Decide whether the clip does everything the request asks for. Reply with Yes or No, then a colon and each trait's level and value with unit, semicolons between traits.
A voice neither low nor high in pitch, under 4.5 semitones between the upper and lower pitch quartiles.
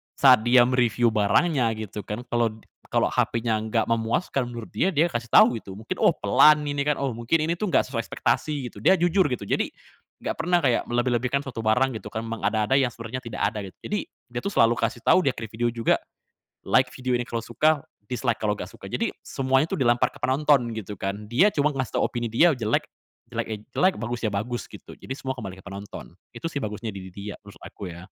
No: low, 120 Hz; average, 3.4 semitones